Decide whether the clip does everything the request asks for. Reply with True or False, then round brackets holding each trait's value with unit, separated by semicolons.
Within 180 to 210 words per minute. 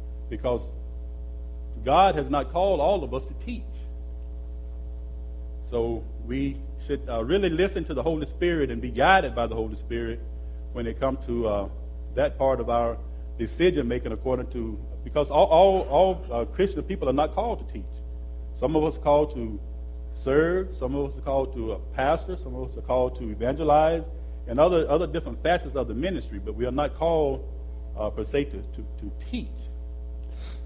True (185 wpm)